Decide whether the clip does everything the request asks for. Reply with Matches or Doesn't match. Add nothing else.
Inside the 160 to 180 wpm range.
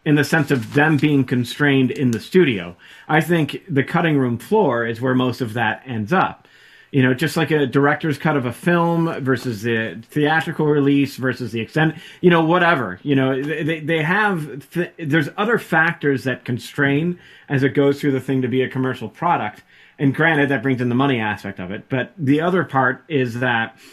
Doesn't match